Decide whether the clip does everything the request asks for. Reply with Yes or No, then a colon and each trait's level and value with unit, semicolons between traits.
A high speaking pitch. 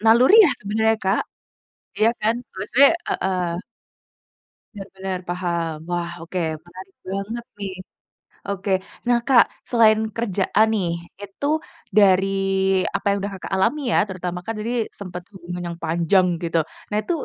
Yes: high, 195 Hz